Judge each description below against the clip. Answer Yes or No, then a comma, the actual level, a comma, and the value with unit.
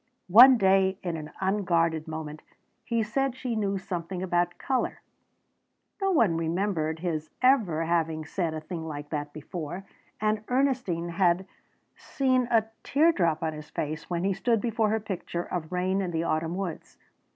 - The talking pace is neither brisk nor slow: Yes, average, 160 wpm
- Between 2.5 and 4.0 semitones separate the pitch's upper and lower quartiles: No, average, 4.9 semitones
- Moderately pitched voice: Yes, medium, 180 Hz